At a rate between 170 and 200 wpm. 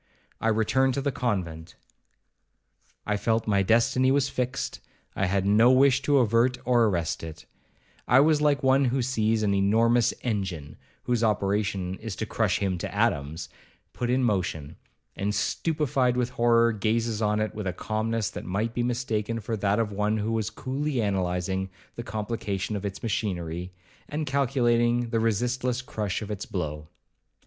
No: average, 155 wpm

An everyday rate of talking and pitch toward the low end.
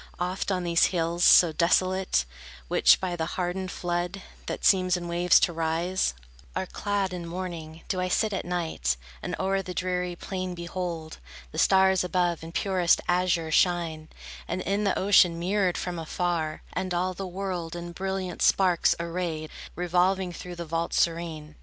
No: average, 165 wpm; medium, 175 Hz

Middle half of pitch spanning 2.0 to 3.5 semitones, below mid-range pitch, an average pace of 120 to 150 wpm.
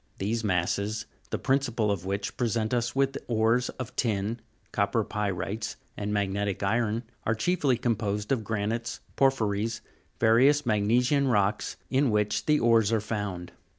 Yes: average, 2.9 semitones; low, 110 Hz; average, 145 wpm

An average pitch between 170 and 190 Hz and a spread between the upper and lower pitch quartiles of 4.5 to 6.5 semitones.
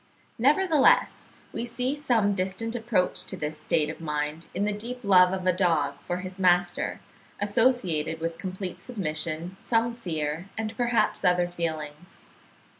Yes: medium, 185 Hz; wide, 5.4 semitones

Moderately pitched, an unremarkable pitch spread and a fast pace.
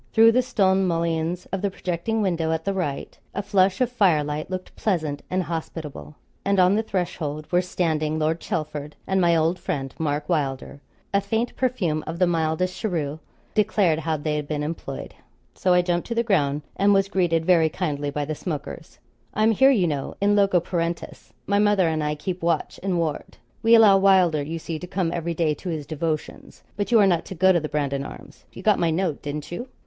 Yes: medium, 170 Hz; average, 3.8 semitones; fast, 210 wpm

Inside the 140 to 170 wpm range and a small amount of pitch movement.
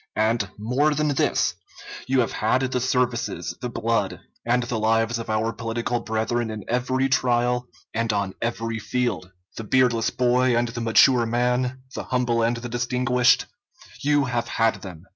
Yes: average, 160 wpm; narrow, 1.8 semitones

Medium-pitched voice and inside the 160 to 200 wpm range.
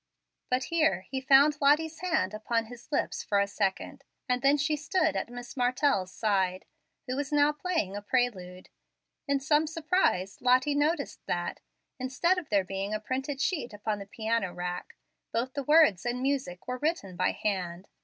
No: very high, 250 Hz; average, 175 wpm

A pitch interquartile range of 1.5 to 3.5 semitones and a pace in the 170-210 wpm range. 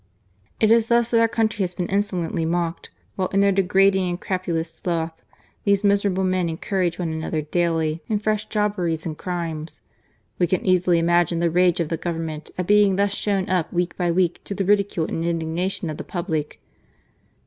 Yes: average, 3.1 semitones; average, 190 wpm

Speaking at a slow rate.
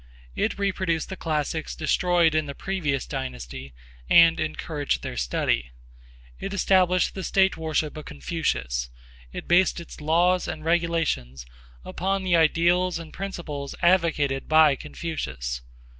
Yes: slow, 130 wpm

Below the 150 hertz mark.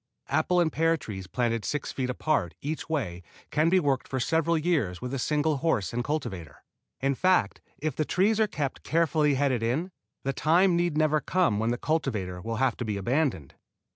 Yes: medium, 140 Hz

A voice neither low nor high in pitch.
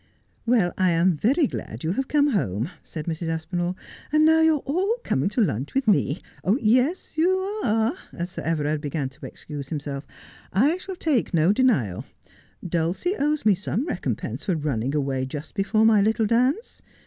No: high, 195 Hz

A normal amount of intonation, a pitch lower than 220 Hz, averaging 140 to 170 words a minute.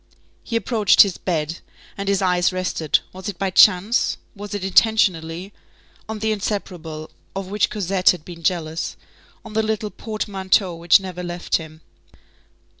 Yes: average, 3.1 semitones; high, 190 Hz; average, 150 wpm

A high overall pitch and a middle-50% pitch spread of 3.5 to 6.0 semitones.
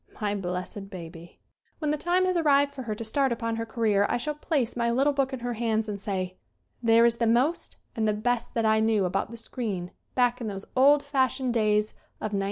Yes: high, 230 Hz; average, 3.8 semitones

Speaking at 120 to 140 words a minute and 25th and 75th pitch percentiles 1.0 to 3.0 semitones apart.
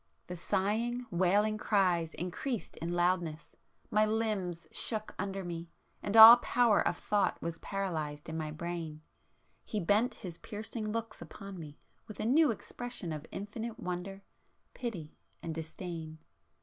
No: slow, 135 wpm; average, 4.4 semitones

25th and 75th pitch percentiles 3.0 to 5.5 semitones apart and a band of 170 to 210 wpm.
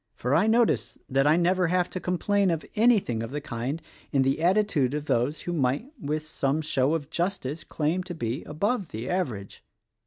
Yes: average, 5.2 semitones; average, 190 wpm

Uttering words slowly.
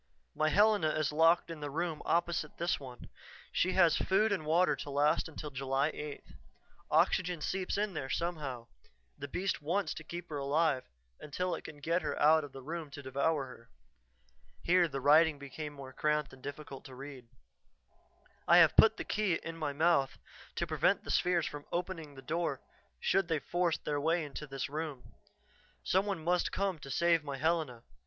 No: average, 185 wpm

